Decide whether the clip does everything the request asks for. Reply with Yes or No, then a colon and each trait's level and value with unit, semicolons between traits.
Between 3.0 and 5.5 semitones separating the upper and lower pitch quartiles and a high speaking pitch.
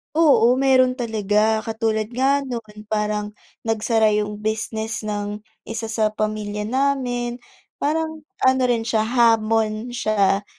No: narrow, 2.5 semitones; high, 220 Hz